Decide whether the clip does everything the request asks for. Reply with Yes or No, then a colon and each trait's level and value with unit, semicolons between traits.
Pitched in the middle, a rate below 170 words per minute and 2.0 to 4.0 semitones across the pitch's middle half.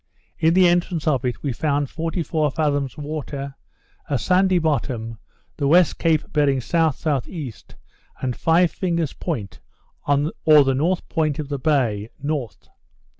Yes: medium, 150 Hz; slow, 135 wpm; average, 3.3 semitones